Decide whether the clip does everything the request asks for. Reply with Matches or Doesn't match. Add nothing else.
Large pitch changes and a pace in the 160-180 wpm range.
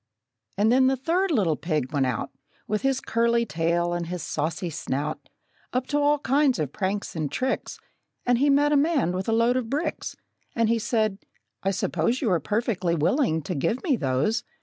Doesn't match